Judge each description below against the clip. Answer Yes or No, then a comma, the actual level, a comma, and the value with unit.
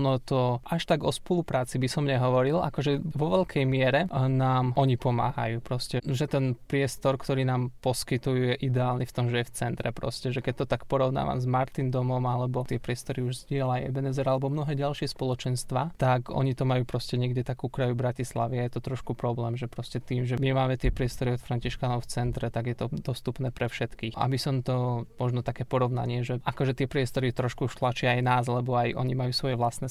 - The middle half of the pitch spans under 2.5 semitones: Yes, narrow, 1.5 semitones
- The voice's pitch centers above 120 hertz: Yes, low, 130 Hz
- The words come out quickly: Yes, fast, 205 wpm